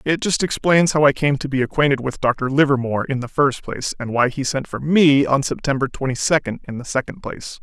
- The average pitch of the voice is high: No, low, 135 Hz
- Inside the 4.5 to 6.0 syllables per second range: Yes, 5.8 syllables/s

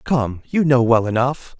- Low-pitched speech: Yes, low, 125 Hz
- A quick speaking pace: No, average, 190 wpm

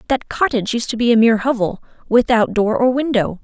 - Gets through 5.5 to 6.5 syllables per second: Yes, 6.0 syllables/s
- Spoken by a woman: Yes, female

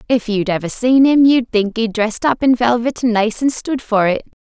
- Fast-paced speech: Yes, fast, 240 wpm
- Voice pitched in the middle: No, high, 235 Hz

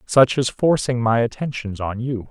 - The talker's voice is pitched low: Yes, low, 120 Hz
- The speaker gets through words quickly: No, average, 180 wpm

